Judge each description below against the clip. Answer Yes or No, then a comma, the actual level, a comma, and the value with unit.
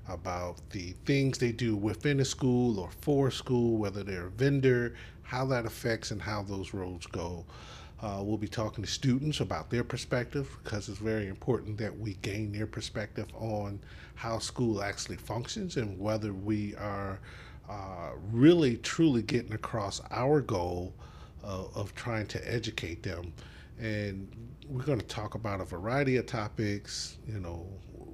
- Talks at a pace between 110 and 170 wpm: Yes, average, 160 wpm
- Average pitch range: Yes, average, 3.7 semitones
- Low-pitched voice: Yes, low, 110 Hz